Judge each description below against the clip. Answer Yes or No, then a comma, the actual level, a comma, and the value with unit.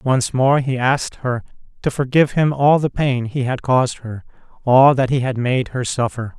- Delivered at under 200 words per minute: No, fast, 205 wpm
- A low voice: Yes, low, 130 Hz